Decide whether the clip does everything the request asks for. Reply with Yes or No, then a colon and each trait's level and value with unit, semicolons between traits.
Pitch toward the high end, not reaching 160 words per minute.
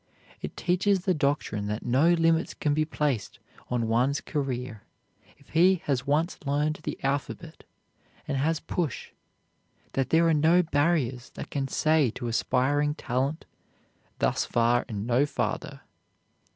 No: medium, 145 Hz; average, 140 wpm